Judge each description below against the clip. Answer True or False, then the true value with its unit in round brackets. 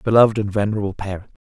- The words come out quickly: False (170 wpm)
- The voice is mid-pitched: False (105 Hz)